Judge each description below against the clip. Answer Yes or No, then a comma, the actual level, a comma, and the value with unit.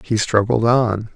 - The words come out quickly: No, average, 155 wpm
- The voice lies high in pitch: No, low, 110 Hz